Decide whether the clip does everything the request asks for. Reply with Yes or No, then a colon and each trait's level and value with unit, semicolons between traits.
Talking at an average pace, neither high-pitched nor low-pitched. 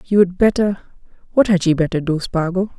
Yes: average, 150 wpm; medium, 180 Hz